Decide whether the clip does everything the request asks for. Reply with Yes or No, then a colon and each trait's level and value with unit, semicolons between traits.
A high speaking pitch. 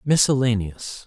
No: low, 120 Hz